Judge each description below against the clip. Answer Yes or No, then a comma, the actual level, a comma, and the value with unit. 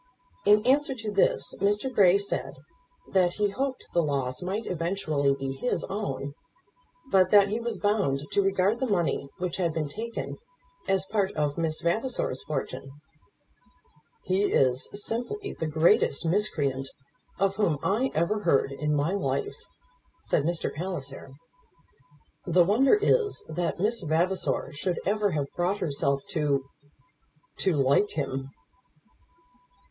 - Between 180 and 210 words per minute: No, slow, 135 wpm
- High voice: No, medium, 180 Hz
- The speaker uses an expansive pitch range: Yes, wide, 5.8 semitones